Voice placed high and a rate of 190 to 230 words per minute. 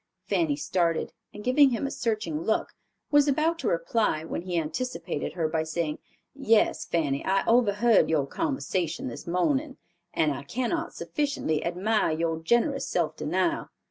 No: high, 195 Hz; average, 150 wpm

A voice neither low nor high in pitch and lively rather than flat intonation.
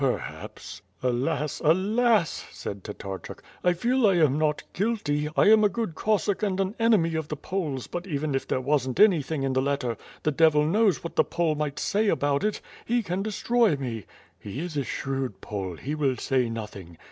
Yes: medium, 155 Hz; wide, 6.6 semitones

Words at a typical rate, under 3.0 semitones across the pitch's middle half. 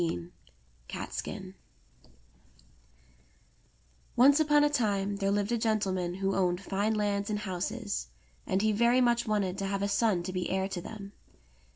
Yes: average, 150 wpm; narrow, 2.5 semitones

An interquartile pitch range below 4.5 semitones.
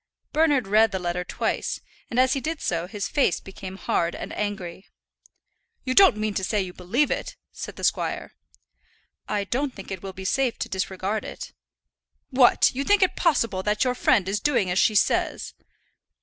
No: average, 5.3 semitones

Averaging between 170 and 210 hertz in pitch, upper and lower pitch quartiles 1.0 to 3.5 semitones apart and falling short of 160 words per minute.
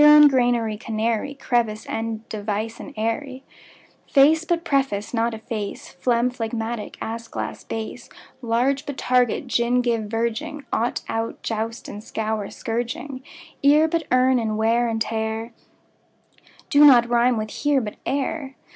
No: high, 235 Hz; average, 3.2 semitones; average, 145 wpm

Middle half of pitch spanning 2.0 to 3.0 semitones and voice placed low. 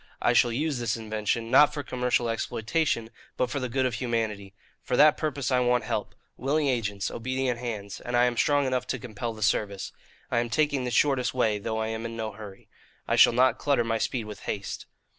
Yes: average, 2.7 semitones; low, 120 Hz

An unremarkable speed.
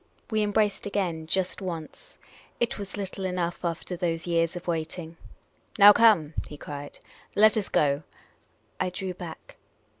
Yes: average, 160 wpm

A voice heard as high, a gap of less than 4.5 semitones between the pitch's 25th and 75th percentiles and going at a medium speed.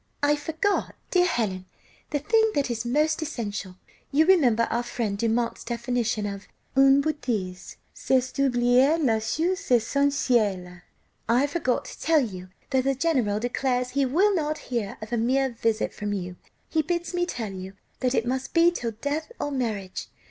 No: very high, 250 Hz; average, 5.0 semitones; average, 165 wpm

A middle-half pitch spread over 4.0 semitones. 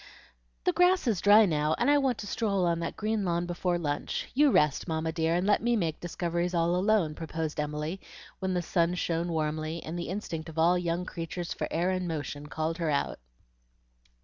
No: average, 2.8 semitones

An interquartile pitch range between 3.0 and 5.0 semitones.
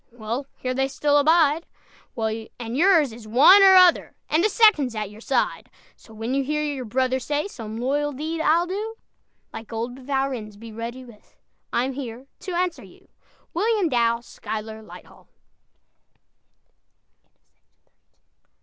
No: wide, 5.5 semitones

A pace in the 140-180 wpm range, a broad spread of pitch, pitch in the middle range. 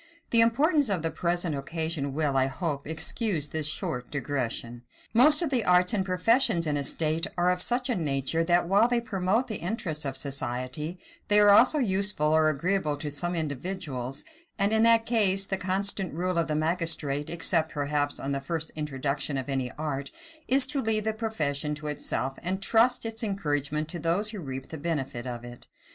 No: average, 190 wpm; wide, 5.7 semitones; medium, 165 Hz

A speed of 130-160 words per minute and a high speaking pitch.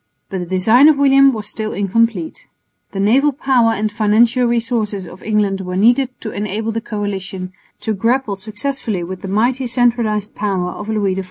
No: average, 175 wpm; high, 215 Hz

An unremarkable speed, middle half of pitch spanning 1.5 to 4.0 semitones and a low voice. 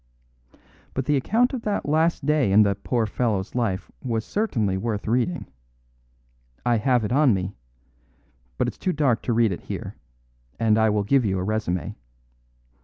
No: average, 170 wpm; average, 5.1 semitones; low, 115 Hz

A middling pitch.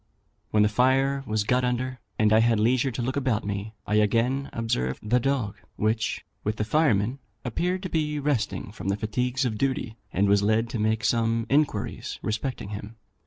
No: low, 115 Hz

